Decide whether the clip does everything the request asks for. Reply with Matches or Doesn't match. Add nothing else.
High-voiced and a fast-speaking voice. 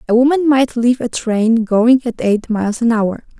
Matches